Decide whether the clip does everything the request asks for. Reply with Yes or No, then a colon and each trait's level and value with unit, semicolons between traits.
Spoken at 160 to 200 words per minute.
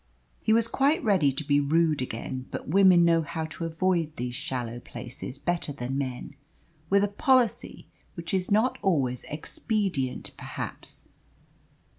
No: average, 145 wpm